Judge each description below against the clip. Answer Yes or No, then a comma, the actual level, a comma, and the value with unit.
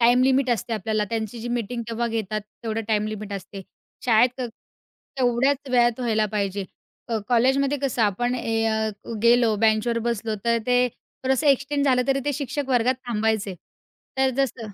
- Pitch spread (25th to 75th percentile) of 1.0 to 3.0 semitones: Yes, narrow, 2.6 semitones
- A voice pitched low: No, high, 235 Hz